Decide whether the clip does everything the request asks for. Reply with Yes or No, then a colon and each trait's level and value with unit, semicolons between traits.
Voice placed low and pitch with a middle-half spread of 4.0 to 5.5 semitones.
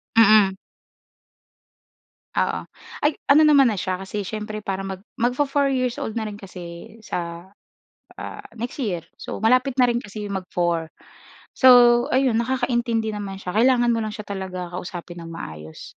No: high, 215 Hz; average, 4.6 semitones